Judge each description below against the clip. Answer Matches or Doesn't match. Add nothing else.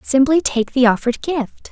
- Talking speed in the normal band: Matches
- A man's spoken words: Doesn't match